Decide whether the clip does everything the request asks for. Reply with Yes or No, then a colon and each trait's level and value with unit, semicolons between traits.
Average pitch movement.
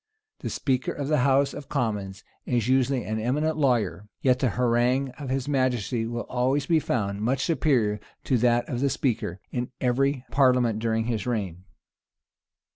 Yes: average, 3.1 semitones